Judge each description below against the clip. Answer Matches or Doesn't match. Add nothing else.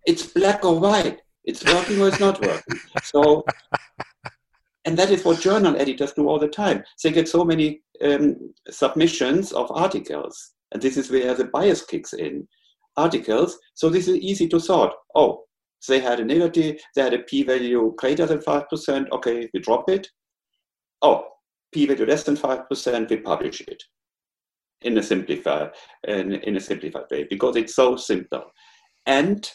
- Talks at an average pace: Matches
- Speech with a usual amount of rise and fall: Doesn't match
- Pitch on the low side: Doesn't match